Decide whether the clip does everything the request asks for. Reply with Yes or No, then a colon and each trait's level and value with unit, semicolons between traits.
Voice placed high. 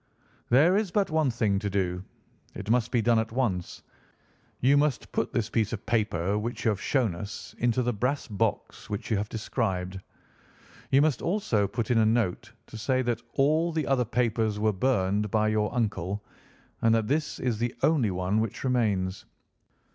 No: low, 115 Hz